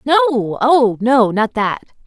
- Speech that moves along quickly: No, average, 145 wpm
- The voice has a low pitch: No, high, 240 Hz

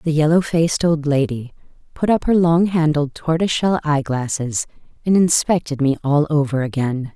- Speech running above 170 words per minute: No, average, 160 wpm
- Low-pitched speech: No, medium, 155 Hz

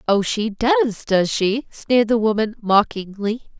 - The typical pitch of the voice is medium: No, high, 220 Hz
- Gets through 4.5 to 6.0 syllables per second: No, 4.0 syllables/s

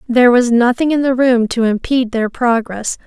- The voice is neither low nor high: No, high, 240 Hz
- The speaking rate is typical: Yes, average, 195 wpm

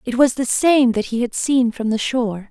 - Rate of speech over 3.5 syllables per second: Yes, 5.0 syllables/s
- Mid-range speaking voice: No, high, 245 Hz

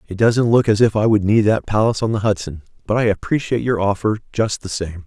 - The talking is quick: Yes, fast, 250 wpm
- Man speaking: Yes, male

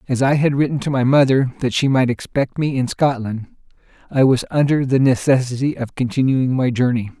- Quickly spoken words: No, average, 190 wpm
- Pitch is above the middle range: No, low, 130 Hz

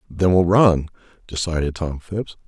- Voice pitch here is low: Yes, very low, 85 Hz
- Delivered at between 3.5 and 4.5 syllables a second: Yes, 4.4 syllables/s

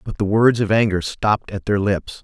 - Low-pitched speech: Yes, low, 105 Hz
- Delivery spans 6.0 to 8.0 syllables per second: No, 5.2 syllables/s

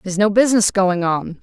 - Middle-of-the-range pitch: No, high, 195 Hz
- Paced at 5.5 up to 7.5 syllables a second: Yes, 6.0 syllables/s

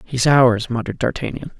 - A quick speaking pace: No, average, 150 wpm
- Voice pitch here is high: No, low, 125 Hz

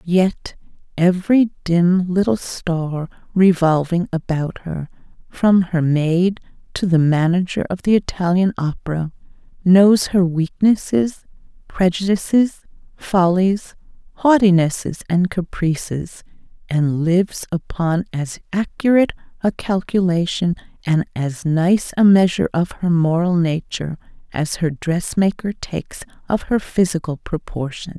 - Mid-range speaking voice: Yes, medium, 180 Hz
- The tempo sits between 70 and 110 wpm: Yes, slow, 105 wpm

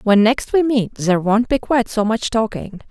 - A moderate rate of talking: No, fast, 225 wpm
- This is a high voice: Yes, high, 225 Hz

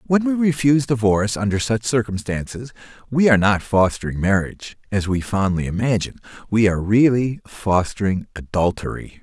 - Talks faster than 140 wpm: No, slow, 135 wpm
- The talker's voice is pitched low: Yes, low, 110 Hz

